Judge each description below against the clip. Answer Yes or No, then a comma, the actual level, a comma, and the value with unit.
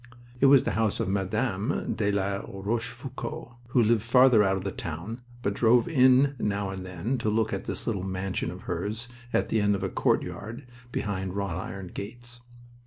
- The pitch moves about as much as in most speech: Yes, average, 3.7 semitones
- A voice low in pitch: Yes, low, 105 Hz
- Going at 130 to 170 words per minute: No, average, 185 wpm